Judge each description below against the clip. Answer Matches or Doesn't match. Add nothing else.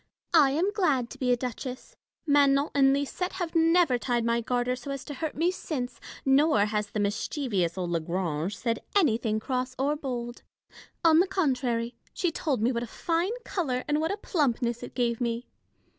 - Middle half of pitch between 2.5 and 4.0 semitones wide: Doesn't match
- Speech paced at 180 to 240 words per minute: Matches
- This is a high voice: Matches